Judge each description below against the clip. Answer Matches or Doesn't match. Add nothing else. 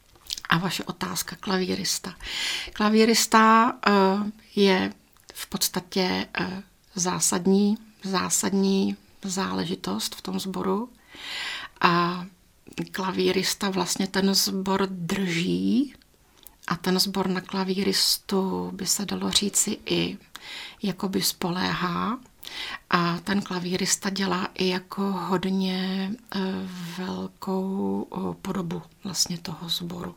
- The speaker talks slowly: Matches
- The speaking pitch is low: Doesn't match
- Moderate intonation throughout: Doesn't match